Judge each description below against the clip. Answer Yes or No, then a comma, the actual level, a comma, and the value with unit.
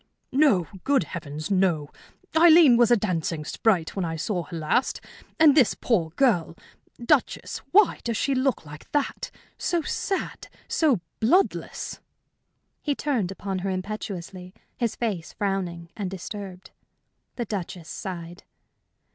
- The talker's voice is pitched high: Yes, high, 195 Hz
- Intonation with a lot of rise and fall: Yes, wide, 6.7 semitones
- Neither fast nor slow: No, slow, 130 wpm